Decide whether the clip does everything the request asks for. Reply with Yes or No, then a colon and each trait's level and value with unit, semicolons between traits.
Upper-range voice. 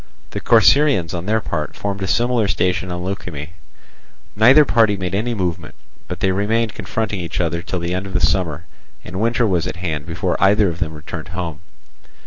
No: very low, 90 Hz